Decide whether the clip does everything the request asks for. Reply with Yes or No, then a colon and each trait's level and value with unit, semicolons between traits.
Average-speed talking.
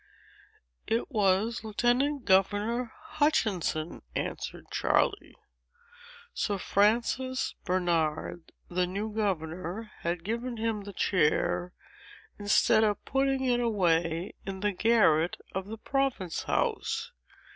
No: slow, 105 wpm